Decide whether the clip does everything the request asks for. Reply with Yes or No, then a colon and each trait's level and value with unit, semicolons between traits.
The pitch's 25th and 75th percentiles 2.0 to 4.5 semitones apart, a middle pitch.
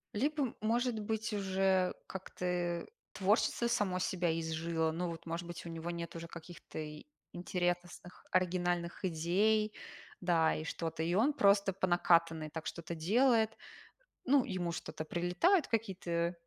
Yes: average, 3.6 semitones; medium, 180 Hz